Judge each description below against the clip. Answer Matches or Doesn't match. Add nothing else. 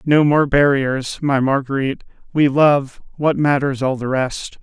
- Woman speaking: Doesn't match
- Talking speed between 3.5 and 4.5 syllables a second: Matches